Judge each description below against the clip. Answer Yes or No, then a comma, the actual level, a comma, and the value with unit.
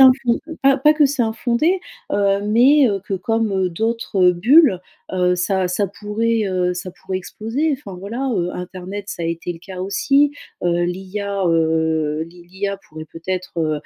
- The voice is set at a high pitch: Yes, high, 195 Hz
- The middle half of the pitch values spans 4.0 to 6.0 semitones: Yes, average, 4.4 semitones